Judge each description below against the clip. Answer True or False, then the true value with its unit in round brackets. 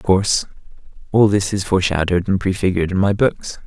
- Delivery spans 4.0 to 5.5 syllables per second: False (6.5 syllables/s)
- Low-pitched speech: True (95 Hz)